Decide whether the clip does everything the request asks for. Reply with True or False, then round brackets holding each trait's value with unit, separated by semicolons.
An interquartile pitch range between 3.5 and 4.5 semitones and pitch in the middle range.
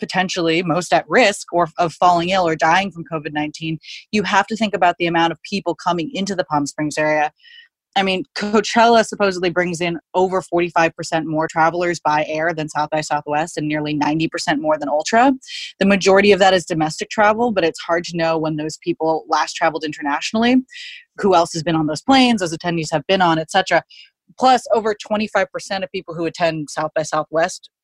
True (3.8 semitones; 175 Hz)